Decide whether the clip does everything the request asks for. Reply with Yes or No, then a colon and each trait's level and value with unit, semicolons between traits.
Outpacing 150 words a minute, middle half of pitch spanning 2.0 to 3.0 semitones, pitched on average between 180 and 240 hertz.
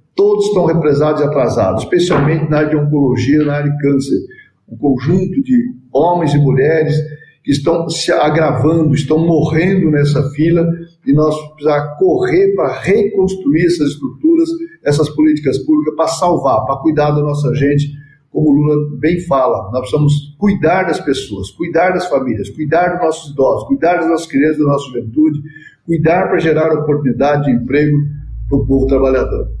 No: average, 160 wpm; narrow, 2.5 semitones; medium, 150 Hz